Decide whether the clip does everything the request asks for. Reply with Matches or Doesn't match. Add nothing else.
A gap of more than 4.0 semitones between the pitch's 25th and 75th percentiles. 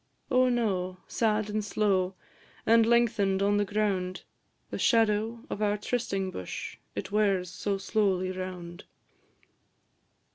Doesn't match